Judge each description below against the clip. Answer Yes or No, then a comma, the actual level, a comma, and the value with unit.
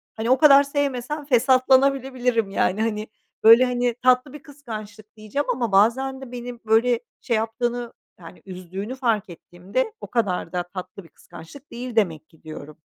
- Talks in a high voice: Yes, high, 235 Hz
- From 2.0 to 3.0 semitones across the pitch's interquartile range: No, average, 4.2 semitones